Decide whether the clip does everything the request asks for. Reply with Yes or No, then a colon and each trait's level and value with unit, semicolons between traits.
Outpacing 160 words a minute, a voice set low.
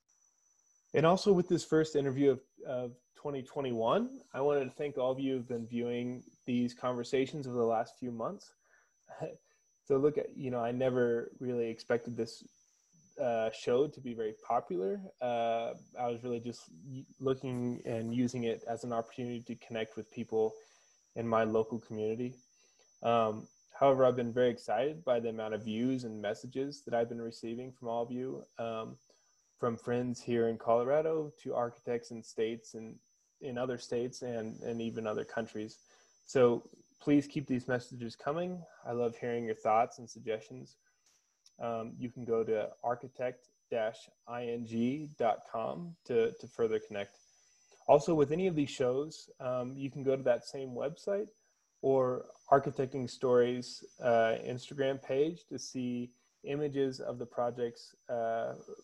No: average, 155 wpm; low, 125 Hz